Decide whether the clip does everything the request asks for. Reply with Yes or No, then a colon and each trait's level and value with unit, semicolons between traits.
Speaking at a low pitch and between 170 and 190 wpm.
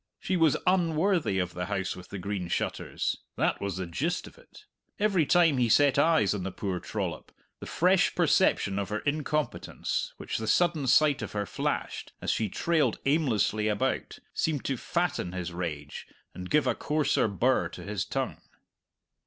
Yes: low, 125 Hz; average, 175 wpm